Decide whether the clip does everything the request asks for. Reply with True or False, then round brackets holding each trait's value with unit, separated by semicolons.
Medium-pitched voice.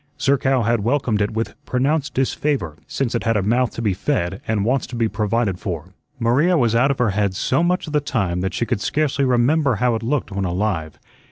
False (115 Hz)